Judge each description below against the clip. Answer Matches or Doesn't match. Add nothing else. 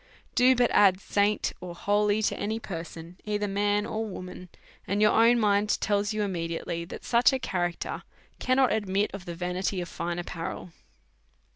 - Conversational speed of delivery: Matches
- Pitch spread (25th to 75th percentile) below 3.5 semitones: Matches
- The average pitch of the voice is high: Matches